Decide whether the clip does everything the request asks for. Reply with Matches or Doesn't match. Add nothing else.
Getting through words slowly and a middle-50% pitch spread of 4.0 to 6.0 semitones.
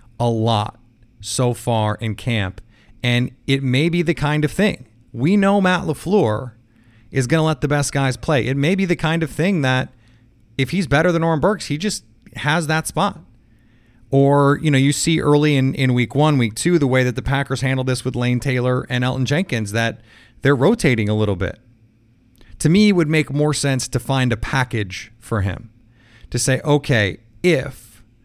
Doesn't match